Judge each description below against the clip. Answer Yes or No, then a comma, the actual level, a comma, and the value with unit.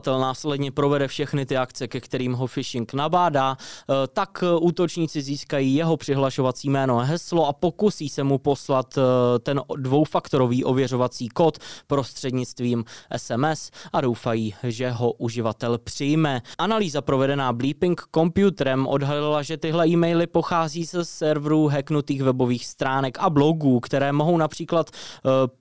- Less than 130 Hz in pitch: No, medium, 140 Hz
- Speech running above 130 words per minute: No, average, 125 wpm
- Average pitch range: Yes, average, 3.6 semitones